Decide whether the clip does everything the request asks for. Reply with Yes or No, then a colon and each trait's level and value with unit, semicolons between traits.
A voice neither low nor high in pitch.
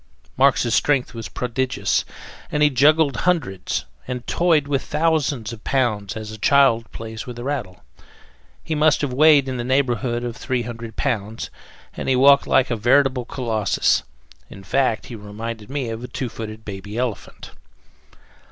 No: low, 125 Hz